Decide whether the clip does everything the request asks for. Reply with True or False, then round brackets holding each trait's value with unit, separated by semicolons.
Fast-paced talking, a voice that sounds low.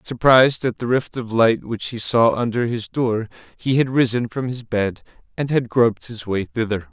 True (210 wpm; 115 Hz)